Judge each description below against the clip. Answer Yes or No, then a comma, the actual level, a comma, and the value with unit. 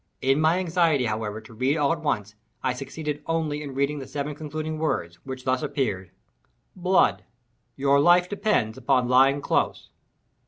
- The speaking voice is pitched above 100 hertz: Yes, medium, 140 Hz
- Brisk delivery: No, average, 150 wpm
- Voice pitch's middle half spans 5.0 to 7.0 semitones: No, average, 4.3 semitones